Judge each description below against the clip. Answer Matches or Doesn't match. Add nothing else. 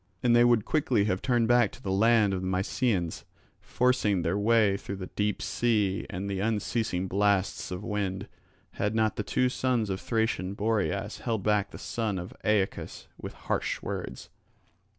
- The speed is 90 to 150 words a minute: Doesn't match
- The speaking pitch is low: Matches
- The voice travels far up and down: Doesn't match